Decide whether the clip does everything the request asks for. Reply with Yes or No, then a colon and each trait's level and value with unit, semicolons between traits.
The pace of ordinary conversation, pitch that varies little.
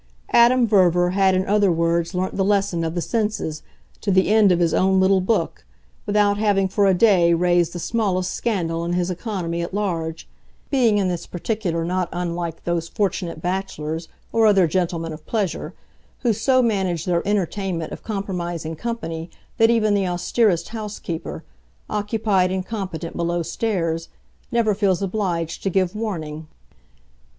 No: average, 160 wpm; average, 3.4 semitones